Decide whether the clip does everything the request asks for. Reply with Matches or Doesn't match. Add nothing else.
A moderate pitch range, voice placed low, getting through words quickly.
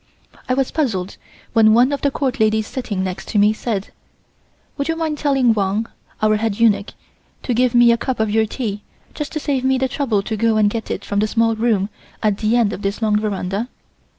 Doesn't match